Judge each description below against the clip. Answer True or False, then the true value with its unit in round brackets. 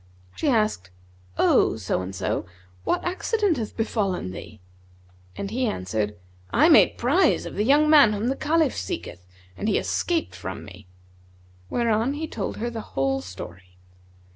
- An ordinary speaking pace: True (155 wpm)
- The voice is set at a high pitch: True (215 Hz)